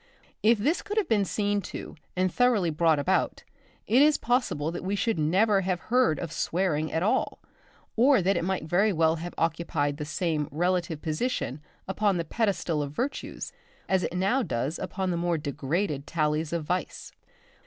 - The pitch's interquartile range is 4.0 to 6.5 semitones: Yes, average, 4.6 semitones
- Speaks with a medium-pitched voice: Yes, medium, 180 Hz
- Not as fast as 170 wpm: No, average, 175 wpm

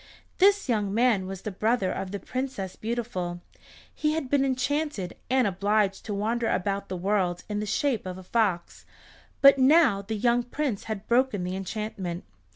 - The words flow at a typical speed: Yes, average, 170 wpm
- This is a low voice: No, high, 215 Hz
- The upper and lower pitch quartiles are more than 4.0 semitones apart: Yes, average, 4.7 semitones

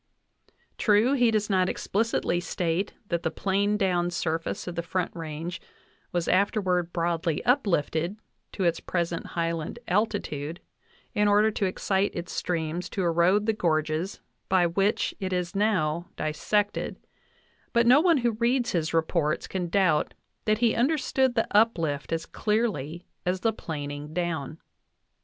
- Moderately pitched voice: Yes, medium, 180 Hz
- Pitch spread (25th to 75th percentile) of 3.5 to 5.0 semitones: Yes, average, 4.1 semitones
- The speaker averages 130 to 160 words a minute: Yes, average, 145 wpm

